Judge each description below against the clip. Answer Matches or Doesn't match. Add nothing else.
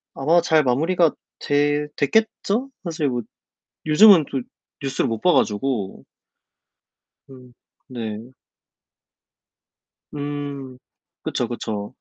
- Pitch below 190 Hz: Matches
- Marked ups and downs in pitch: Doesn't match